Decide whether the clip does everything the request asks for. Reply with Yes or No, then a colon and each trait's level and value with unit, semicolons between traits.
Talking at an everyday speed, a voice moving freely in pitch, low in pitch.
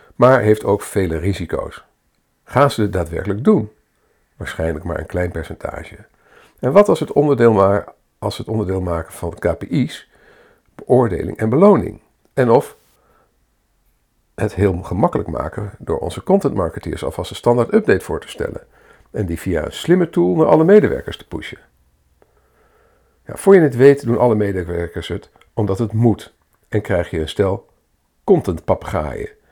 Yes: average, 150 wpm; wide, 7.6 semitones; low, 105 Hz